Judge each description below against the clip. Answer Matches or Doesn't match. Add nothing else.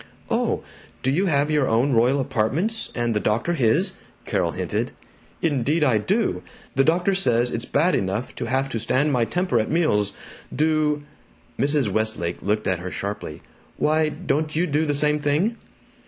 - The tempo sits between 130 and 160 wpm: Doesn't match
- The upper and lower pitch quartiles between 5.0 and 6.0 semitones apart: Matches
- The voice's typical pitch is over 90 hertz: Matches